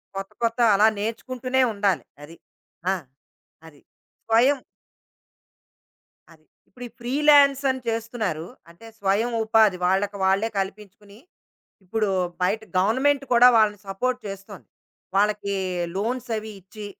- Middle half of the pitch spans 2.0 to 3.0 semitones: No, average, 3.8 semitones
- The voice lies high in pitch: Yes, high, 215 Hz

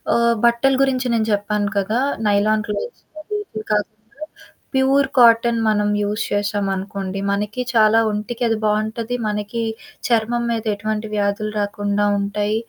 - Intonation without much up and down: Yes, narrow, 2.2 semitones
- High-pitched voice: Yes, high, 215 Hz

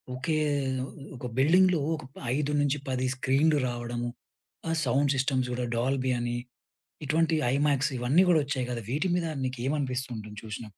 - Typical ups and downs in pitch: Yes, average, 3.3 semitones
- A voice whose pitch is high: No, low, 135 Hz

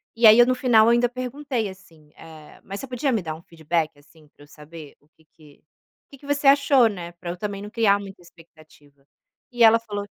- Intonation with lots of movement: Yes, wide, 7.0 semitones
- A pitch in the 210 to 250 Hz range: No, high, 200 Hz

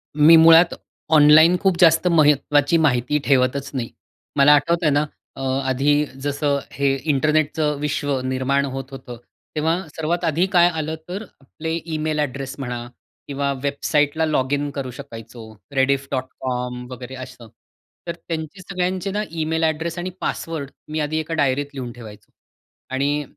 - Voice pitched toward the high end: No, medium, 145 Hz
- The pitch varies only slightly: No, average, 3.2 semitones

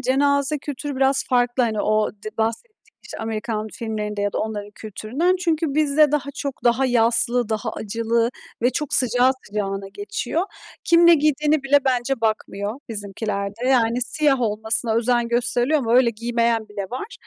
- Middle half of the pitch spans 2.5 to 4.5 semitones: Yes, average, 4.1 semitones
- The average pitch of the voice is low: No, high, 240 Hz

